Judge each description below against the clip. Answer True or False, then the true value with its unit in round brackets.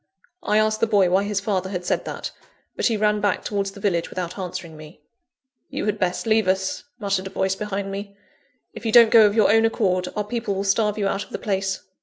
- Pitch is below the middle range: False (200 Hz)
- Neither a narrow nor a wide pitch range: False (1.9 semitones)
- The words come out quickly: True (235 wpm)